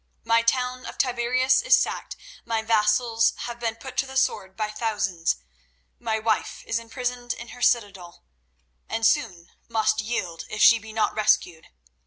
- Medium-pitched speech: No, high, 225 Hz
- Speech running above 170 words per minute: No, average, 160 wpm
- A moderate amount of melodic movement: No, narrow, 2.3 semitones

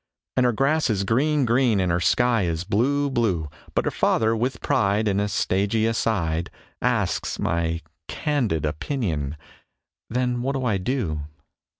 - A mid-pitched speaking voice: No, low, 110 Hz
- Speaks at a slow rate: No, average, 155 wpm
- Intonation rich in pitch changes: Yes, wide, 6.2 semitones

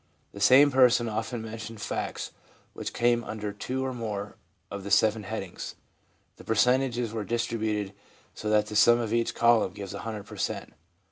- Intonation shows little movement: Yes, narrow, 2.2 semitones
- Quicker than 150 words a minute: Yes, average, 165 wpm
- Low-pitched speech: Yes, low, 110 Hz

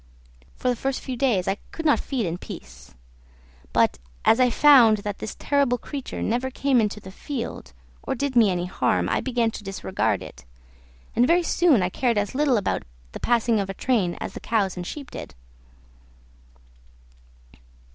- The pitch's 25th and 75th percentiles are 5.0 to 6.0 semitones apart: Yes, average, 5.3 semitones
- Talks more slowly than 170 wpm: No, average, 175 wpm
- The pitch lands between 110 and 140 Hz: No, high, 235 Hz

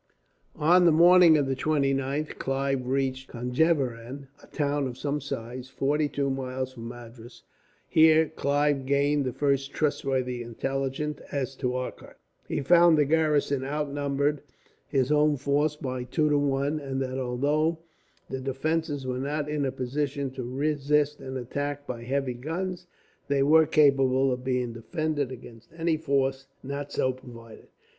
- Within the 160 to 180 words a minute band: No, average, 150 wpm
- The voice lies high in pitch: No, medium, 140 Hz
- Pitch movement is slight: Yes, narrow, 2.3 semitones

